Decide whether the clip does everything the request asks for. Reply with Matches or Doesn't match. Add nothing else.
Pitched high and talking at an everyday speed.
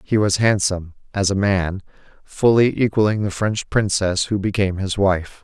Doesn't match